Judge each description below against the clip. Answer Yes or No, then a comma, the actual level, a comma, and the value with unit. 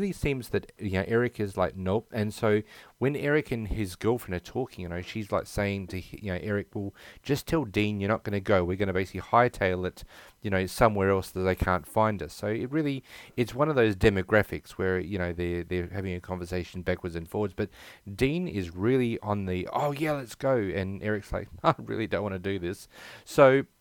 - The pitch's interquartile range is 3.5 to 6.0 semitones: Yes, average, 3.9 semitones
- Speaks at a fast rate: Yes, fast, 230 wpm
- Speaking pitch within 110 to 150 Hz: No, low, 100 Hz